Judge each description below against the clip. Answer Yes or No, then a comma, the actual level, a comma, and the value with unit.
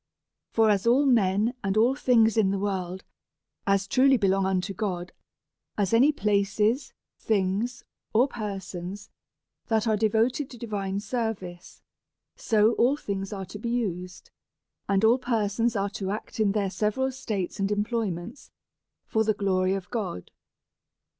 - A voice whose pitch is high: Yes, high, 210 Hz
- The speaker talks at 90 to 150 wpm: Yes, average, 145 wpm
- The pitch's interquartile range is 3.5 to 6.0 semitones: No, average, 3.0 semitones